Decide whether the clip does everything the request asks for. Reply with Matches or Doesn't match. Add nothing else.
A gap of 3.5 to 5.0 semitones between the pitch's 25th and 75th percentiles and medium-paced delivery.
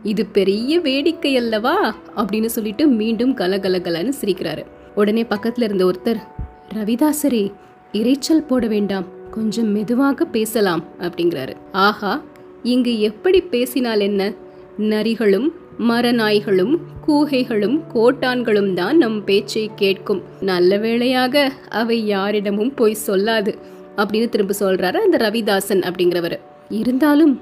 Matches